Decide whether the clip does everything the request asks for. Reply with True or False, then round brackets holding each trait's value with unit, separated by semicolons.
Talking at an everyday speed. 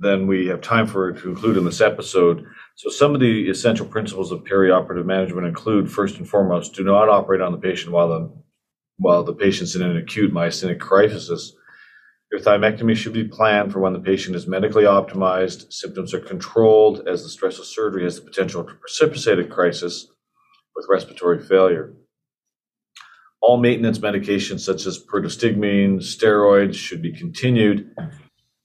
True (170 wpm)